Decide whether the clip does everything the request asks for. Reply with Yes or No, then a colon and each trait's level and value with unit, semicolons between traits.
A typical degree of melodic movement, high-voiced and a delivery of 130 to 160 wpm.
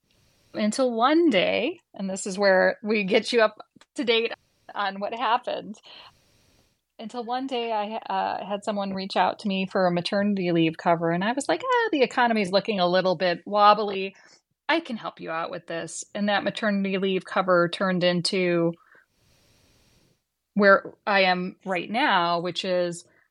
No: average, 3.6 semitones; high, 200 Hz; average, 170 wpm